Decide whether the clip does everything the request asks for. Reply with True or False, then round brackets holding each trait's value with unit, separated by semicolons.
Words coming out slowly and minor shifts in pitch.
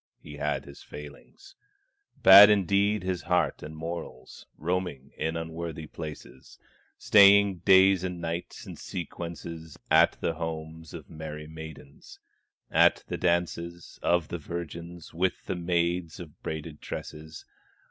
True (125 wpm; 2.2 semitones)